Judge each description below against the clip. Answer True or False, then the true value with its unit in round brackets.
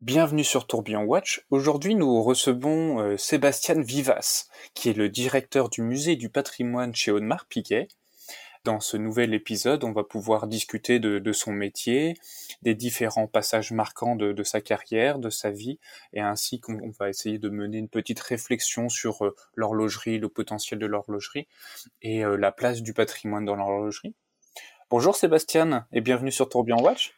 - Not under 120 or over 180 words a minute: True (170 wpm)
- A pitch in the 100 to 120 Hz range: True (115 Hz)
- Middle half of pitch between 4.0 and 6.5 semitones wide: False (3.2 semitones)